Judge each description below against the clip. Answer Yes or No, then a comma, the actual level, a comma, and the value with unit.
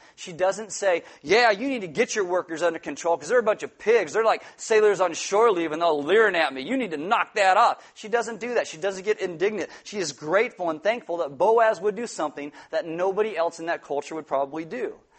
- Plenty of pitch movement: Yes, wide, 5.9 semitones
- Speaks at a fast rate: Yes, fast, 245 wpm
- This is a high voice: Yes, high, 195 Hz